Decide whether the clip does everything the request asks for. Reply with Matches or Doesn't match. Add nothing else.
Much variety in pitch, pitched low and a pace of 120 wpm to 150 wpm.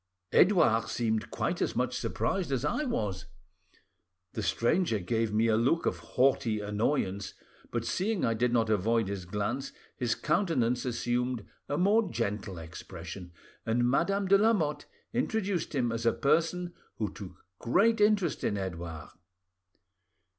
Matches